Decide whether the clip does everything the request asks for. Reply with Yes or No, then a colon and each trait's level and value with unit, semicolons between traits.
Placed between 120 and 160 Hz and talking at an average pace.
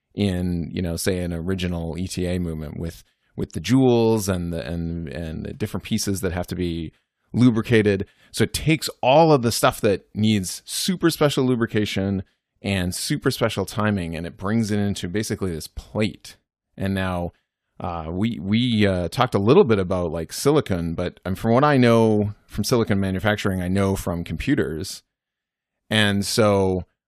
No: low, 100 Hz; average, 165 wpm